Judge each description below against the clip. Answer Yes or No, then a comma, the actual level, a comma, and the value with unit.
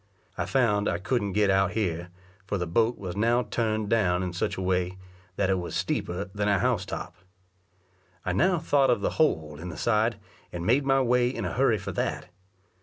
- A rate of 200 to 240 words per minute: Yes, fast, 205 wpm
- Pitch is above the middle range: No, low, 105 Hz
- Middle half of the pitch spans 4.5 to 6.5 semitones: Yes, average, 4.9 semitones